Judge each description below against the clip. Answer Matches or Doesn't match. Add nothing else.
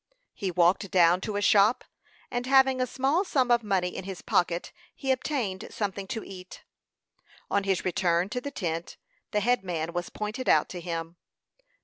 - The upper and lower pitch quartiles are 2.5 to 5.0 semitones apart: Doesn't match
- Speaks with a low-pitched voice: Doesn't match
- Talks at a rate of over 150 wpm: Matches